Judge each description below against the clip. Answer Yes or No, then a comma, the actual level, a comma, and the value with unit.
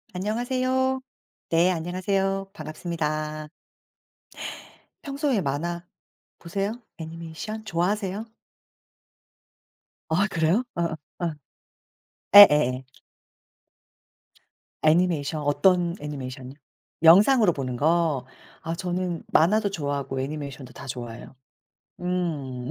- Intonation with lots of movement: No, average, 4.7 semitones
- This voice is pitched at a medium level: Yes, medium, 170 Hz